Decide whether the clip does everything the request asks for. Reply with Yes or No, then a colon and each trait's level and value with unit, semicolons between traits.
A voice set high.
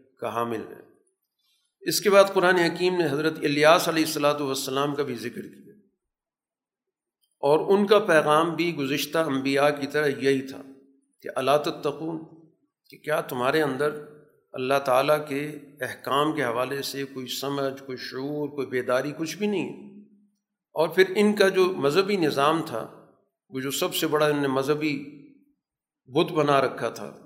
No: medium, 150 Hz